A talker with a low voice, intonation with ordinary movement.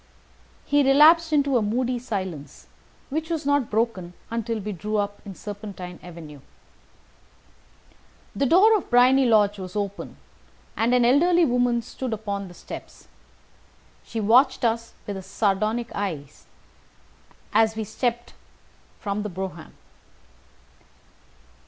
No: high, 225 Hz; average, 4.2 semitones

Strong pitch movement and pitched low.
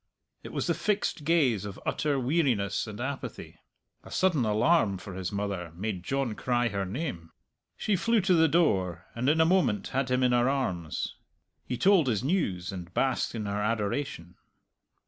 Yes: wide, 7.0 semitones; low, 120 Hz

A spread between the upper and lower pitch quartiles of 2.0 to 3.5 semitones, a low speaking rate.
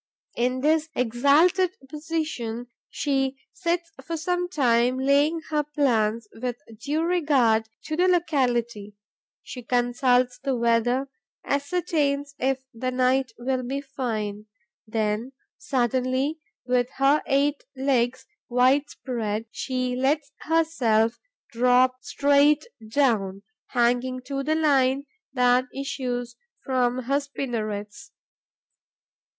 Yes: average, 3.1 semitones; slow, 105 wpm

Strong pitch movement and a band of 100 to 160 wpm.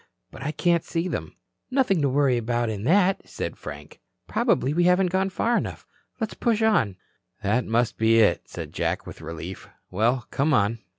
No: wide, 8.5 semitones; average, 180 wpm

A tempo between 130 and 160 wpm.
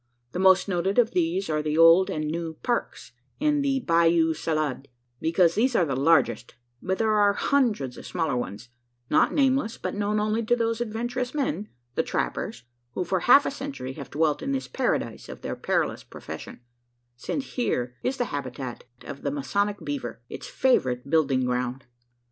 No: average, 175 wpm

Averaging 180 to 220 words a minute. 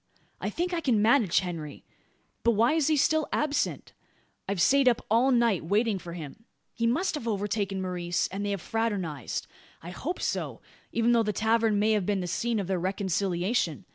Yes: average, 190 wpm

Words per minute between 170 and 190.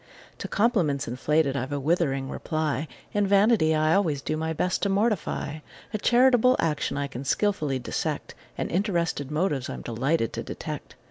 No: average, 160 wpm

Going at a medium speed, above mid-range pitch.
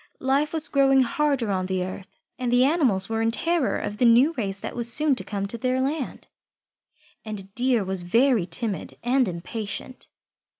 Yes: average, 180 wpm; high, 235 Hz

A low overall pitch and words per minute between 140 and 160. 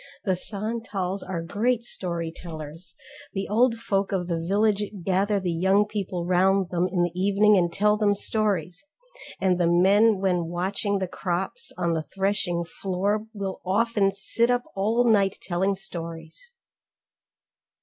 No: high, 195 Hz; average, 150 wpm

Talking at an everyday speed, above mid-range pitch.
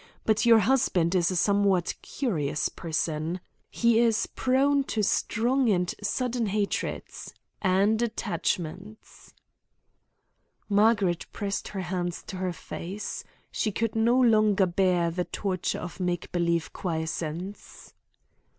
No: slow, 115 wpm; high, 195 Hz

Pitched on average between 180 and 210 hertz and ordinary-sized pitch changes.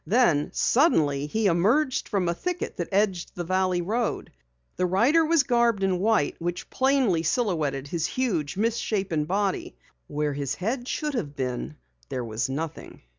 No: medium, 185 Hz; wide, 7.3 semitones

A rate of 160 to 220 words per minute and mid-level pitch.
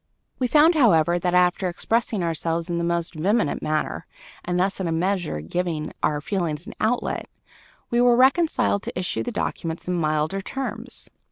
Yes: average, 170 wpm; medium, 180 Hz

